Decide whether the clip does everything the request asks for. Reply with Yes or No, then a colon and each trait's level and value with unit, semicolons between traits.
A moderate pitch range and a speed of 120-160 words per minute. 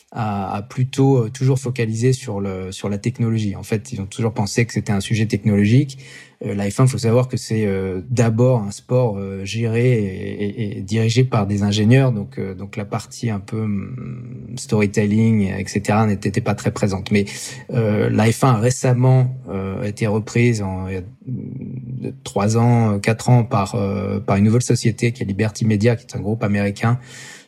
No: average, 3.2 semitones; average, 185 wpm